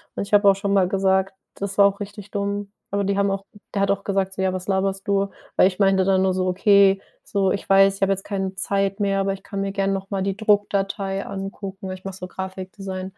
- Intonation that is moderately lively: No, narrow, 0.7 semitones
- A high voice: Yes, high, 195 Hz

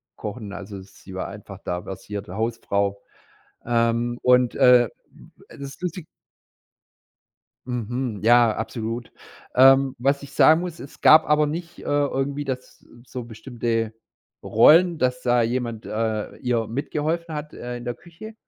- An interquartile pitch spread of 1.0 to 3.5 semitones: No, average, 4.0 semitones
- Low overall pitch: Yes, low, 120 Hz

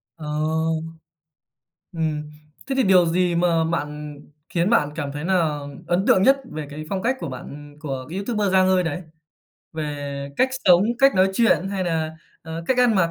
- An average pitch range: Yes, average, 3.9 semitones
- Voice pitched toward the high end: No, medium, 170 Hz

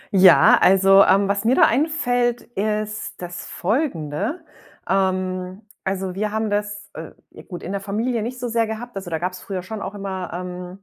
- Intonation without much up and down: No, average, 3.2 semitones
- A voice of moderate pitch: No, high, 200 Hz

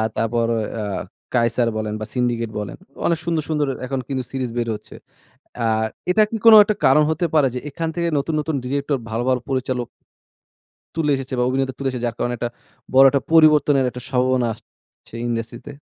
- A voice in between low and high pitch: No, low, 130 Hz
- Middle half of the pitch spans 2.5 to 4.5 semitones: Yes, average, 3.7 semitones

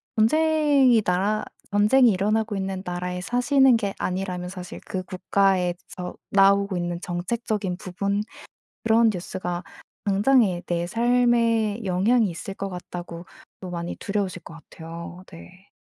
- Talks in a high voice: Yes, high, 195 Hz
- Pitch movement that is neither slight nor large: Yes, average, 3.8 semitones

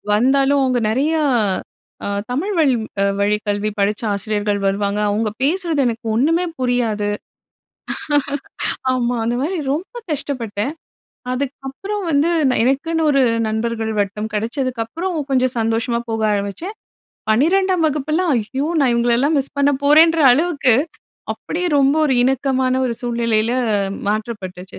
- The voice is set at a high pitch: Yes, very high, 255 Hz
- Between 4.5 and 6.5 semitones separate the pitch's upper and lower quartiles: Yes, average, 5.0 semitones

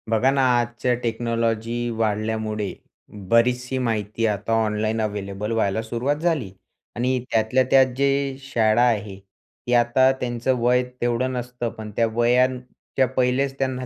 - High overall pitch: No, low, 120 Hz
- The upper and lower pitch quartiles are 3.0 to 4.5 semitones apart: No, narrow, 2.4 semitones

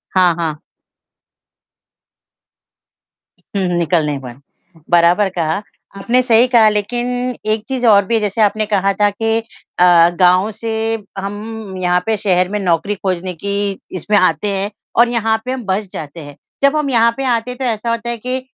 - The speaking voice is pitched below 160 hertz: No, high, 205 Hz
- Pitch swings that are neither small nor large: Yes, average, 4.1 semitones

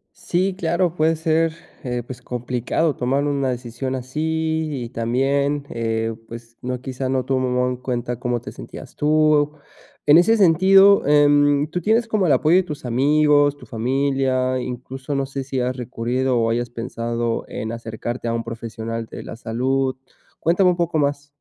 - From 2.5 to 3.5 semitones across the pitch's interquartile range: No, average, 3.9 semitones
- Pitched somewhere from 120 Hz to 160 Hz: Yes, low, 135 Hz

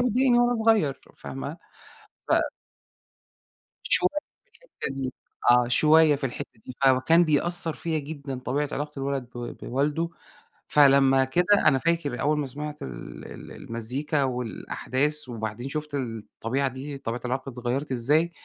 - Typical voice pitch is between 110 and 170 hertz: Yes, medium, 140 Hz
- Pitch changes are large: No, average, 3.3 semitones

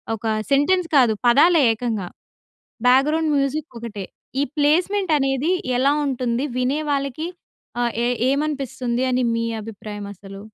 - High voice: Yes, very high, 270 Hz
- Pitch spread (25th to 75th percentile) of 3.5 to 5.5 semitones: Yes, average, 4.1 semitones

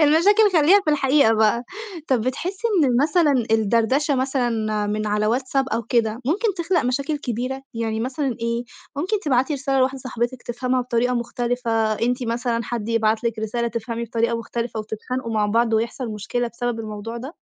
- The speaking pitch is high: Yes, high, 240 Hz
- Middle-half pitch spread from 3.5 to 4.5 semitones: No, average, 2.9 semitones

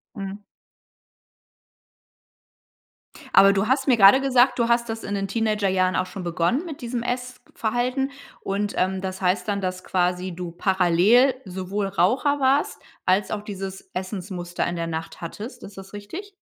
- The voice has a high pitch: Yes, high, 200 Hz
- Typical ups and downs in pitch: Yes, average, 4.6 semitones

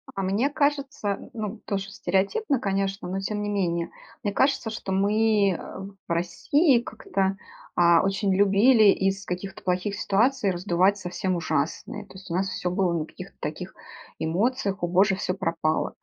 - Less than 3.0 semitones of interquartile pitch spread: Yes, narrow, 2.5 semitones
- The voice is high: Yes, high, 195 Hz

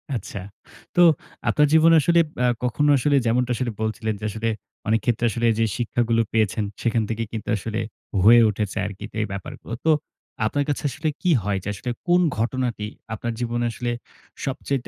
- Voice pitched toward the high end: No, low, 115 Hz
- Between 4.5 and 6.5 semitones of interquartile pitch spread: No, average, 2.9 semitones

